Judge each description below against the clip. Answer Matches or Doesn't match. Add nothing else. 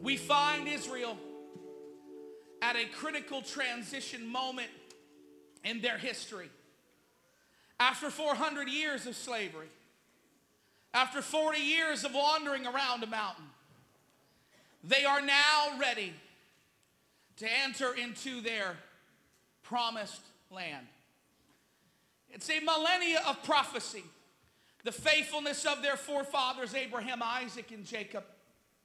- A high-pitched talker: Matches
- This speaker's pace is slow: Matches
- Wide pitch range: Doesn't match